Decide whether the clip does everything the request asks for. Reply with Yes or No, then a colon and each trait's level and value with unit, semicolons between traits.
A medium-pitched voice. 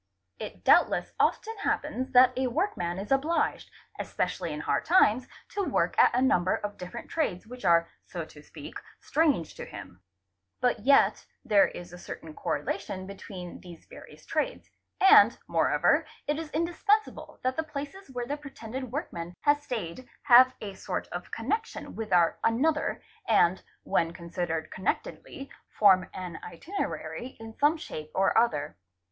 No: high, 235 Hz